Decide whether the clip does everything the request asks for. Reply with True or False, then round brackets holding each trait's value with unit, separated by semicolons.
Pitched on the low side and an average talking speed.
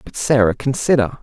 True (120 Hz; 145 wpm)